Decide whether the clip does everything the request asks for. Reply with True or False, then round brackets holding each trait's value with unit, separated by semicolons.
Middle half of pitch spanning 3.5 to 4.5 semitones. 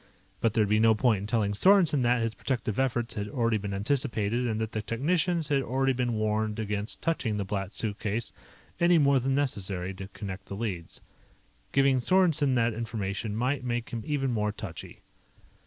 True (4.2 semitones)